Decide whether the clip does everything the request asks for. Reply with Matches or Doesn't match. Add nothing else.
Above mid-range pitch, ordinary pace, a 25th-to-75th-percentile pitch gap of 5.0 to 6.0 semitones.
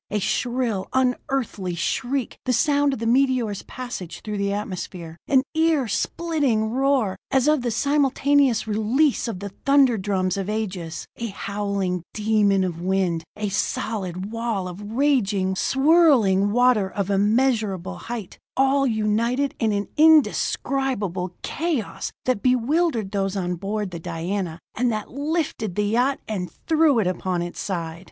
Matches